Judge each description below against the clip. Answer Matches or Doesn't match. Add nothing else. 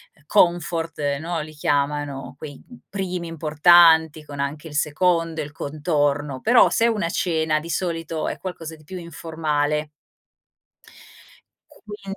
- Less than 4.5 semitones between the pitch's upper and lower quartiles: Matches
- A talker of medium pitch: Matches